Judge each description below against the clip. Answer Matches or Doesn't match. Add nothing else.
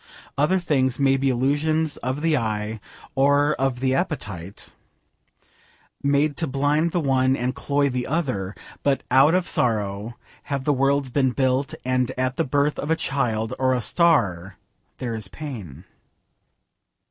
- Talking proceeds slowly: Doesn't match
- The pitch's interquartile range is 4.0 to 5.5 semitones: Doesn't match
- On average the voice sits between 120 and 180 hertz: Matches